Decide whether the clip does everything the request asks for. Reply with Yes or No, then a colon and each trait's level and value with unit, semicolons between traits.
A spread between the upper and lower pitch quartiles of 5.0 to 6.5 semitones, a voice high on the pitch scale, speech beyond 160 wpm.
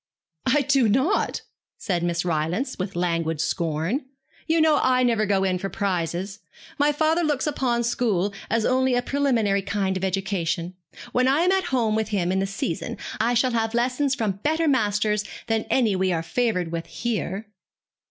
Yes: wide, 5.6 semitones; high, 215 Hz; average, 175 wpm